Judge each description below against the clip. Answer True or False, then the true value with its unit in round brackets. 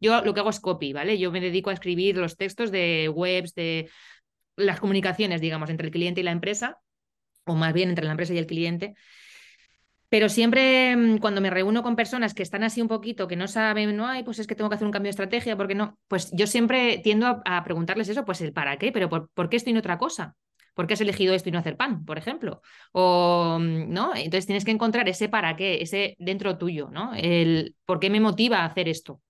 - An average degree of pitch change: True (4.0 semitones)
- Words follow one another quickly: True (240 wpm)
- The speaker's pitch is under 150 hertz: False (195 Hz)